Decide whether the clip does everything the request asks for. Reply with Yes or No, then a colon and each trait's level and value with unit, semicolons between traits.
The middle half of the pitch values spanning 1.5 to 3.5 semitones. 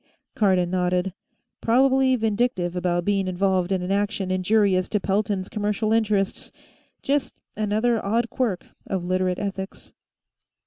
Yes: average, 3.0 semitones